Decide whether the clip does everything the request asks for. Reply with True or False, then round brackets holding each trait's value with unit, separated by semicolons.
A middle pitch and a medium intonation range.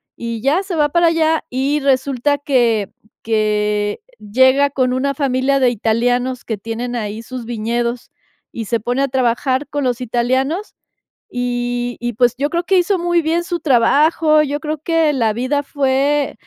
False (260 Hz; 3.7 semitones)